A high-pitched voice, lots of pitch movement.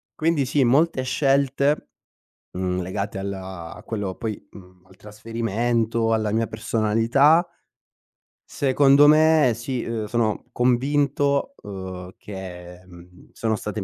No: low, 115 Hz; wide, 6.0 semitones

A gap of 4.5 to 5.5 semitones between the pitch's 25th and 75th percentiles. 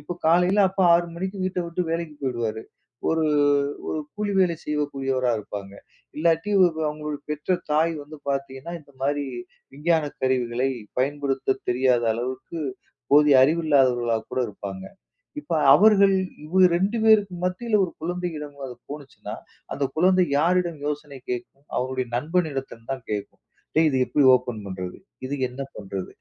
Yes: average, 4.9 semitones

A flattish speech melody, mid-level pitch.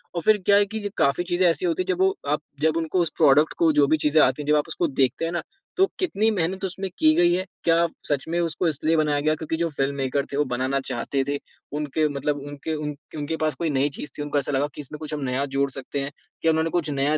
No: average, 3.0 semitones; medium, 155 Hz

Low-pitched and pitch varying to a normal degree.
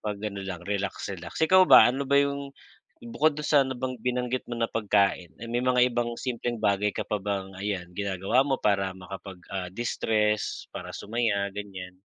Yes: low, 105 Hz; average, 4.3 semitones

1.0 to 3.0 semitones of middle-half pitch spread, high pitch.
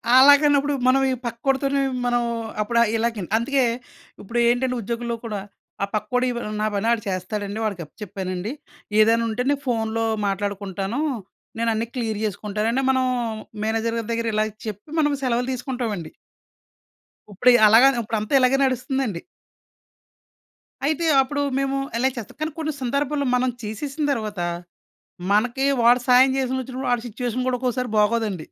No: average, 3.4 semitones; high, 235 Hz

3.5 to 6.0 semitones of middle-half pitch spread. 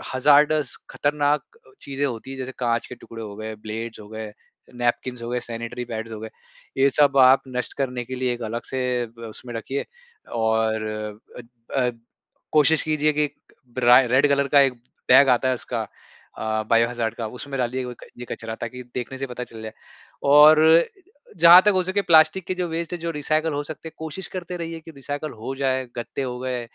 Yes: average, 4.0 semitones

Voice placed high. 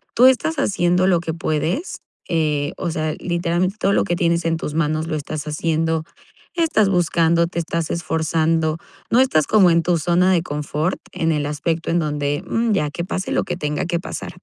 No: medium, 165 Hz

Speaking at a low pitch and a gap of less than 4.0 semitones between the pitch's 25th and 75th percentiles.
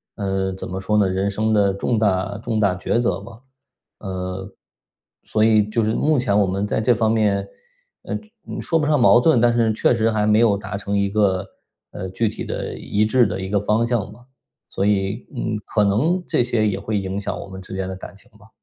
Yes: low, 105 Hz; narrow, 2.6 semitones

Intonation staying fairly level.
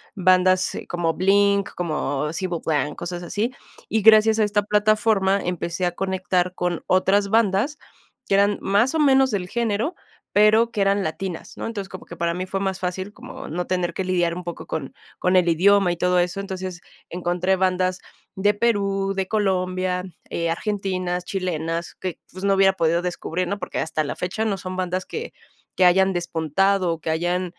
Yes: narrow, 2.3 semitones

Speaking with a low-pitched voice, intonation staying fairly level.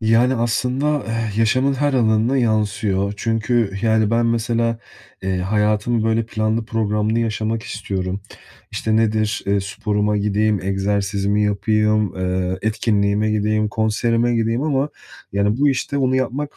Yes: low, 110 Hz; narrow, 2.1 semitones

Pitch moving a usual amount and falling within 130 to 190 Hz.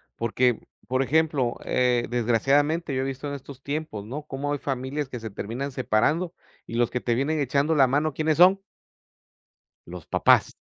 Yes: average, 3.4 semitones; low, 135 Hz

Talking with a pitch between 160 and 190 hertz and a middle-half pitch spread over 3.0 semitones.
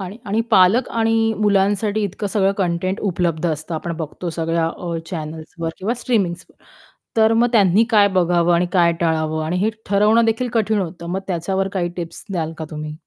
Yes: medium, 185 Hz; average, 3.8 semitones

